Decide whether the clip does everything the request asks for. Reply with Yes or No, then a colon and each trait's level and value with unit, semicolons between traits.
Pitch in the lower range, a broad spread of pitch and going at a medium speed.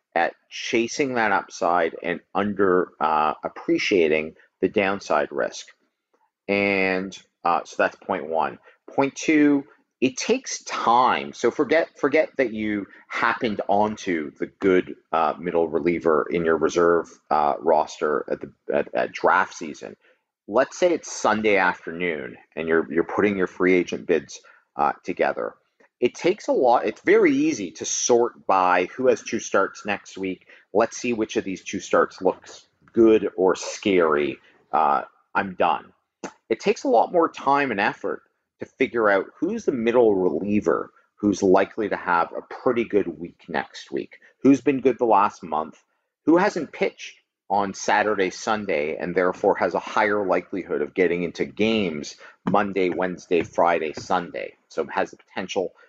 Yes: low, 105 Hz; wide, 7.8 semitones; average, 155 wpm